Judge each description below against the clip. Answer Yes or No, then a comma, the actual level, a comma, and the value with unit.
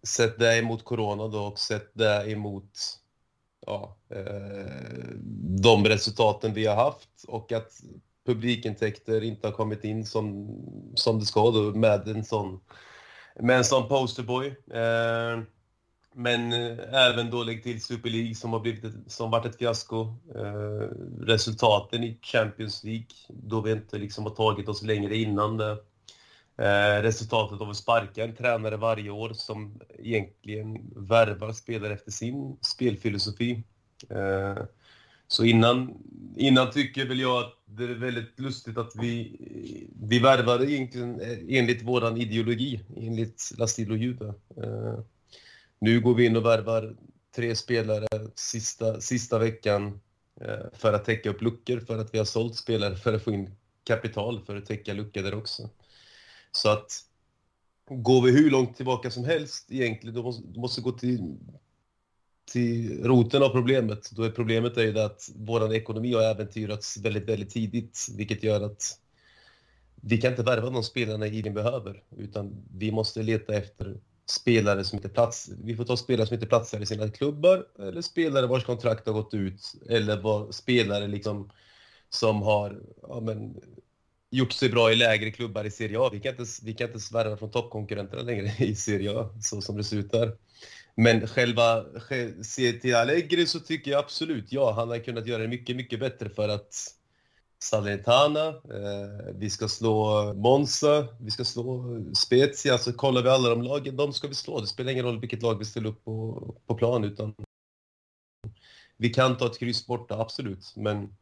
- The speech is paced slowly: No, average, 165 wpm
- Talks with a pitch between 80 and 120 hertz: Yes, low, 115 Hz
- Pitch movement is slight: Yes, narrow, 2.2 semitones